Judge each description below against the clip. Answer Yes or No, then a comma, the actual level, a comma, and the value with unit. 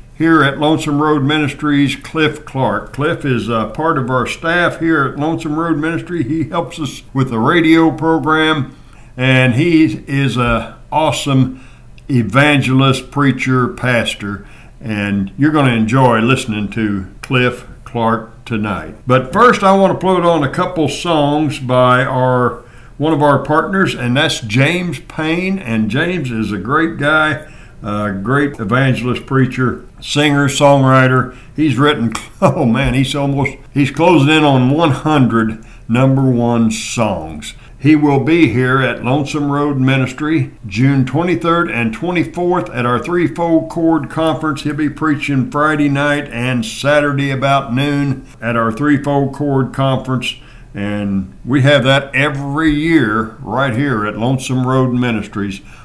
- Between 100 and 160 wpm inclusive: Yes, average, 140 wpm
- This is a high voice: No, low, 135 Hz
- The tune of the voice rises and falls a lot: No, average, 3.8 semitones